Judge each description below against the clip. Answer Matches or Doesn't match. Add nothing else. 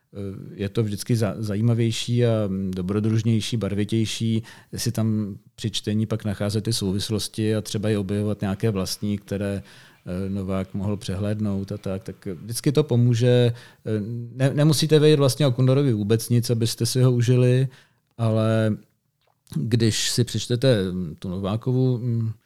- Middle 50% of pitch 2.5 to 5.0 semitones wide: Matches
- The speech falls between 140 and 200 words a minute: Doesn't match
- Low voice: Matches